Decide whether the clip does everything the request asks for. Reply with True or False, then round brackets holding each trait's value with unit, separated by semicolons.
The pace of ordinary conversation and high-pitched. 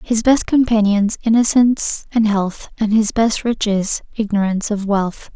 True (145 wpm; 215 Hz)